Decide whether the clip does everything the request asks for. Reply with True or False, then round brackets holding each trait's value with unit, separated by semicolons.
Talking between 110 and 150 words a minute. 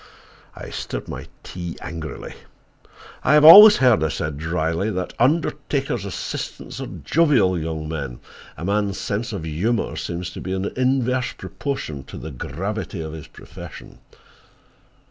True (145 wpm)